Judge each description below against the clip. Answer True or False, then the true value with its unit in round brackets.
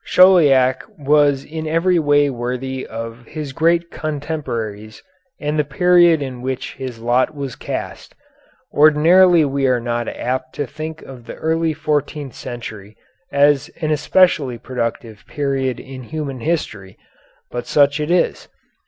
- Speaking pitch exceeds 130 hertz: True (140 Hz)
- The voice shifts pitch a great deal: False (3.7 semitones)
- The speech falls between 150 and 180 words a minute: False (135 wpm)